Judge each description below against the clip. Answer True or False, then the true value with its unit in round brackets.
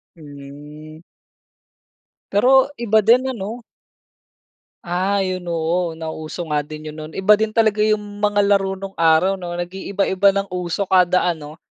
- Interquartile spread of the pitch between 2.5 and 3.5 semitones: False (4.2 semitones)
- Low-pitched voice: False (185 Hz)